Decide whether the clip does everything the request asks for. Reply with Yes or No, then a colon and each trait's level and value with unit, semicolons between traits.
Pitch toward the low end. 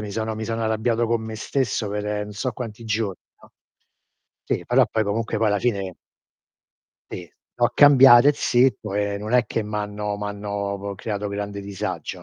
Yes: low, 105 Hz